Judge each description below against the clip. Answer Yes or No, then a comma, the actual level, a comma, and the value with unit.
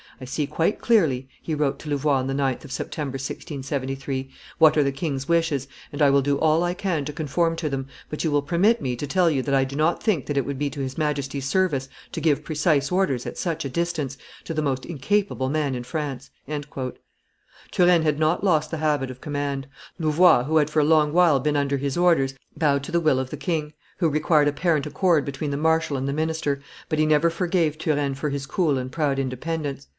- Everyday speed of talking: No, fast, 225 wpm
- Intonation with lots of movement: No, average, 2.8 semitones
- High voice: No, medium, 150 Hz